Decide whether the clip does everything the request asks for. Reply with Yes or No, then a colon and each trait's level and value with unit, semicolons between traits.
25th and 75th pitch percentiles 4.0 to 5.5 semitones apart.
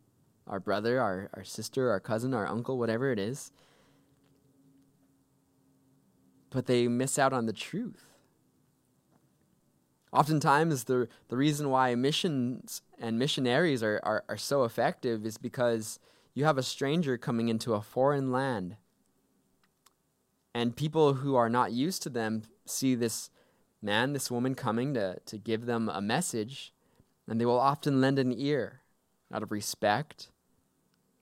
No: average, 3.5 semitones